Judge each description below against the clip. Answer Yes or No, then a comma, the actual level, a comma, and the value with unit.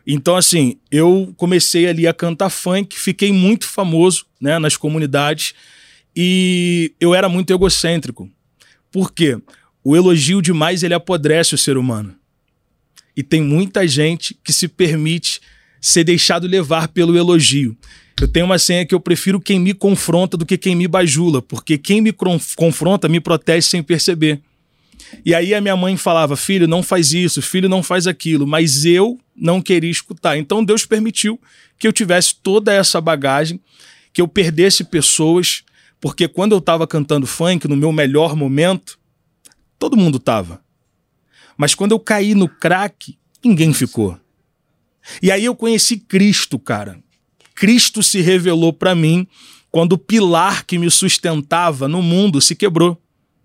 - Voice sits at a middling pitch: Yes, medium, 175 Hz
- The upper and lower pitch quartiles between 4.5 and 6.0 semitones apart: No, average, 3.3 semitones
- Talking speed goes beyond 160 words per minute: No, average, 155 wpm